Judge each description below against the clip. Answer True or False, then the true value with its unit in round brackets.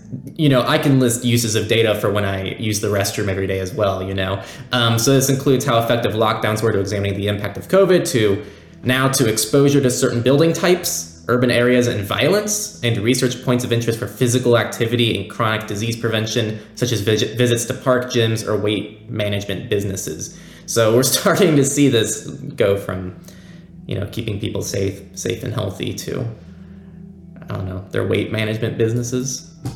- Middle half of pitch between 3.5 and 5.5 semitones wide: True (3.8 semitones)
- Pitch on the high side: False (115 Hz)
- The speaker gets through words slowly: False (185 wpm)